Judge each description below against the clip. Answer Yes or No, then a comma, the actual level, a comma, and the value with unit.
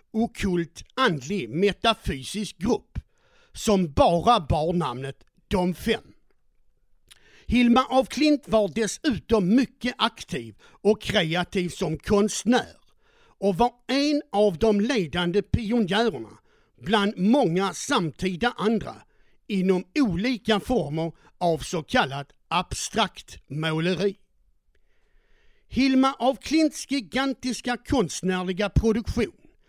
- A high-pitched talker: Yes, high, 215 Hz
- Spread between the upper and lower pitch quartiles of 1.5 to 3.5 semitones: No, wide, 5.4 semitones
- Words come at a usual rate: No, slow, 95 wpm